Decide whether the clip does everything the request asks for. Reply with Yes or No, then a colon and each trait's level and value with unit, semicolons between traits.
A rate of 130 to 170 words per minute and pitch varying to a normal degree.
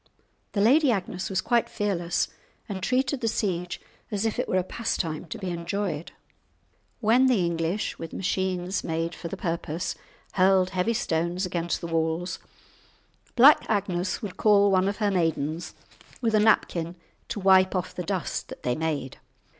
Yes: average, 160 wpm; average, 3.4 semitones